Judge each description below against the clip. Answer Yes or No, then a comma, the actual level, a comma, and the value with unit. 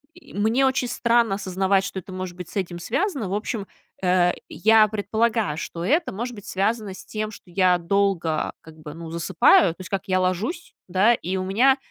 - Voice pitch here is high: Yes, high, 195 Hz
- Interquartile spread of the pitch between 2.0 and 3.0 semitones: No, average, 3.5 semitones